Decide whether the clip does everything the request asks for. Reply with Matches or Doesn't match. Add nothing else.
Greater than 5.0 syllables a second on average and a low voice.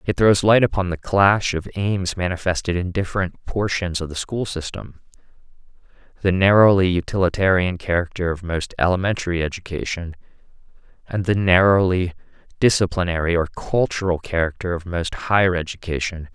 Matches